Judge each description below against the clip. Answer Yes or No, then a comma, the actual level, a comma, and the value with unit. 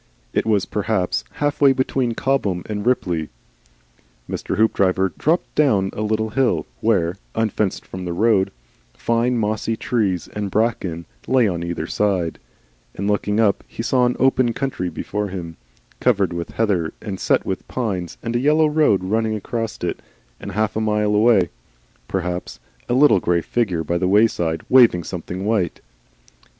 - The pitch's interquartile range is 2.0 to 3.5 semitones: No, average, 4.2 semitones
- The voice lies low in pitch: Yes, low, 105 Hz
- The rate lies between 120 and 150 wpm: No, average, 160 wpm